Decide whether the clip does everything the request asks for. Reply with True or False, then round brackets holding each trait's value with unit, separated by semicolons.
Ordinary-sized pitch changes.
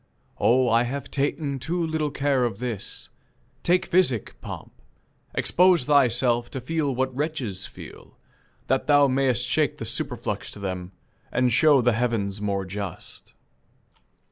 True (4.0 semitones)